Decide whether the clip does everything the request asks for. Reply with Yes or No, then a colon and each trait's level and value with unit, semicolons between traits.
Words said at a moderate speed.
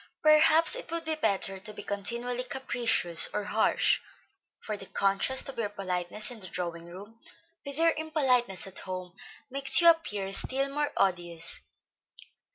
Yes: average, 155 wpm